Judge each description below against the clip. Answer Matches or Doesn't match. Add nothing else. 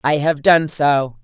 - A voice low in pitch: Doesn't match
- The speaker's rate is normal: Matches